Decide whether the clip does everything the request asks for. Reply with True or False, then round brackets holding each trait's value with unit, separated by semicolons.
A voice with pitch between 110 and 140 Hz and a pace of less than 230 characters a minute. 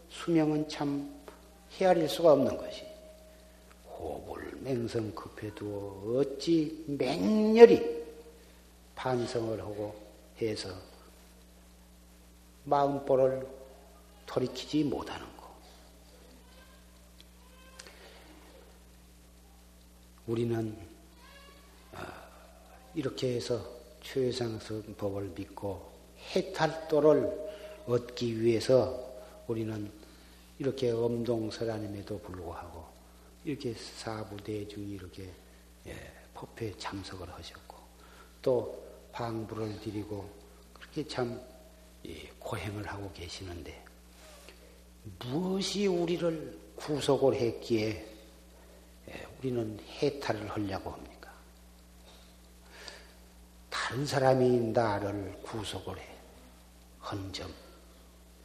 False (100 Hz; 170 characters per minute)